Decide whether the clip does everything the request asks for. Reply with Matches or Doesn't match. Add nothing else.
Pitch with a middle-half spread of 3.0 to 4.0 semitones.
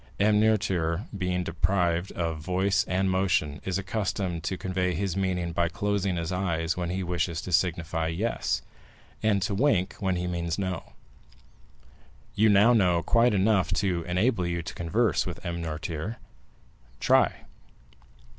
Doesn't match